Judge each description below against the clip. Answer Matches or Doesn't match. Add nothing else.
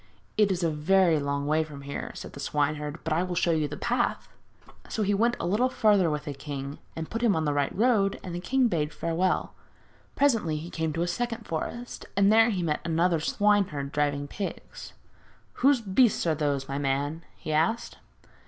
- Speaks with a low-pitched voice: Doesn't match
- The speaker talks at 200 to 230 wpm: Matches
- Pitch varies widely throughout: Matches